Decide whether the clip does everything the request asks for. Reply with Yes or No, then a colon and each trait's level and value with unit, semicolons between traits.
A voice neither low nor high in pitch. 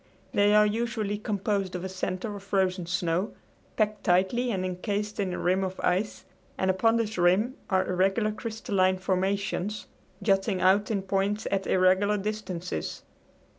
No: high, 195 Hz